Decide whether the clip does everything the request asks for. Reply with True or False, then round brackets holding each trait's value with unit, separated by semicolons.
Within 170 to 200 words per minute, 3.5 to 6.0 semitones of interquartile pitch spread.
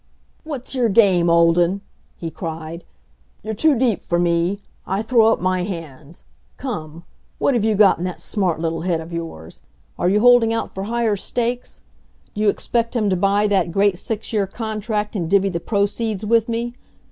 True (180 wpm; 4.7 semitones)